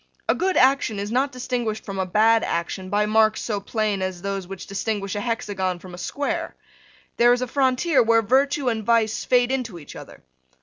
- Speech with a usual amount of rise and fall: Yes, average, 4.2 semitones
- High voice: Yes, high, 220 Hz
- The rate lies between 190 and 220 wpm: Yes, average, 200 wpm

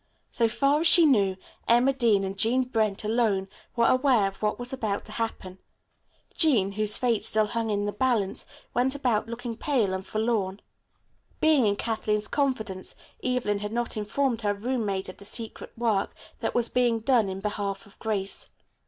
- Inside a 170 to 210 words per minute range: Yes, average, 175 wpm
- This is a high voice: Yes, high, 220 Hz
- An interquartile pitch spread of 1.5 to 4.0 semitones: Yes, average, 3.3 semitones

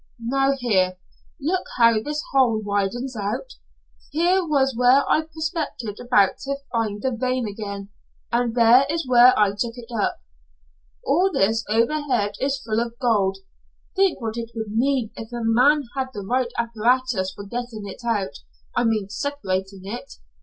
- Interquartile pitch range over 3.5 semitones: Yes, average, 4.1 semitones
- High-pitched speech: Yes, high, 235 Hz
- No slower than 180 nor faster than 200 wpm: No, average, 160 wpm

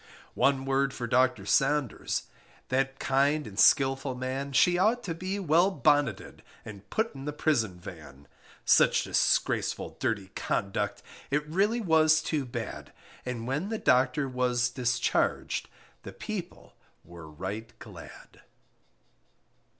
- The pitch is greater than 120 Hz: Yes, low, 135 Hz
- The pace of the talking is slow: Yes, slow, 125 wpm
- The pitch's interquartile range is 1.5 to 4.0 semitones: No, average, 4.7 semitones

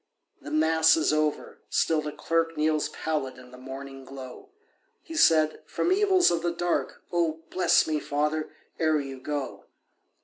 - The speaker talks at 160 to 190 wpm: No, average, 150 wpm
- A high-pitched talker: No, medium, 155 Hz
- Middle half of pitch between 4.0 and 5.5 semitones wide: No, narrow, 2.6 semitones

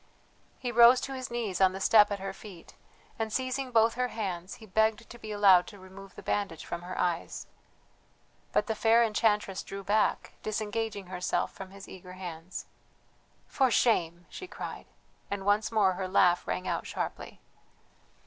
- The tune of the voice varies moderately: Yes, average, 3.2 semitones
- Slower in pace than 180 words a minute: Yes, average, 170 wpm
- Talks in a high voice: Yes, high, 205 Hz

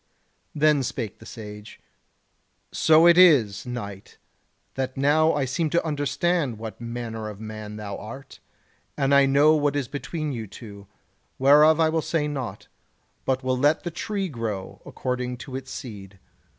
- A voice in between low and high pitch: No, low, 130 Hz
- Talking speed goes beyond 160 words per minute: No, average, 155 wpm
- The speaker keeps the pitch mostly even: No, average, 5.1 semitones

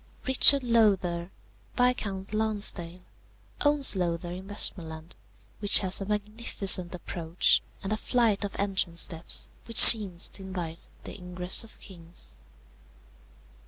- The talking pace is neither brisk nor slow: No, slow, 120 wpm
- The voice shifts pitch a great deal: No, average, 3.6 semitones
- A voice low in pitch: No, high, 190 Hz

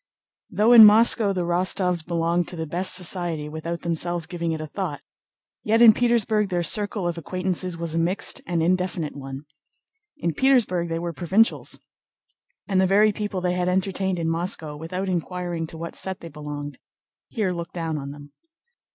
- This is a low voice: No, medium, 175 Hz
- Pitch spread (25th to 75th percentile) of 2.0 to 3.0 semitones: Yes, narrow, 2.5 semitones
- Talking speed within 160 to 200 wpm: Yes, average, 175 wpm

